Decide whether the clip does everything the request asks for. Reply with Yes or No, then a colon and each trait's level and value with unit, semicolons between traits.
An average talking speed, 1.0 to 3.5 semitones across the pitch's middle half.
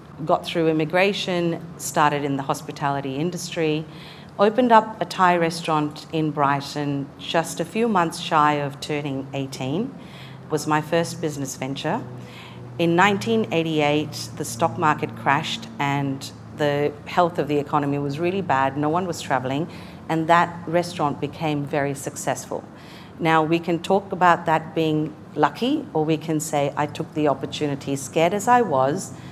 Yes: average, 150 wpm; average, 2.9 semitones